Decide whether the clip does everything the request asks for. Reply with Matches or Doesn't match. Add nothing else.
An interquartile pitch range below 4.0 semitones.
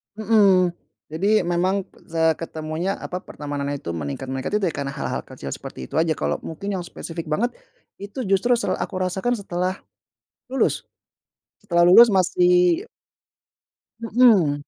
Doesn't match